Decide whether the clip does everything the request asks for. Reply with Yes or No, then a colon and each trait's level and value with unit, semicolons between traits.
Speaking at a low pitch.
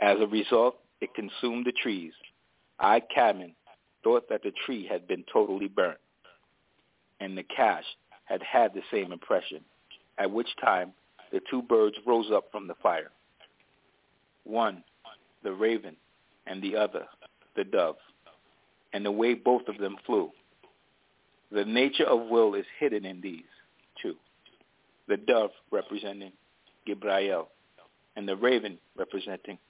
Yes: low, 115 Hz